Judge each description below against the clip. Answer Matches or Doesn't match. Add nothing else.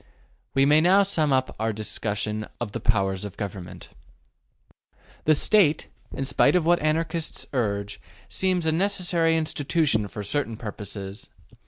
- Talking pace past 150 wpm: Doesn't match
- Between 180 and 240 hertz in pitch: Doesn't match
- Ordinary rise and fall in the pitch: Doesn't match